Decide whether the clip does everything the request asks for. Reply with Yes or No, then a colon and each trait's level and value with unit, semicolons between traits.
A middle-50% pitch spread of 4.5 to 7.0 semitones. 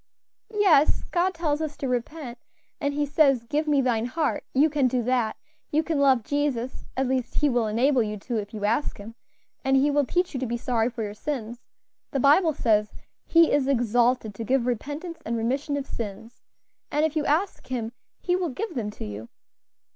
No: average, 4.1 semitones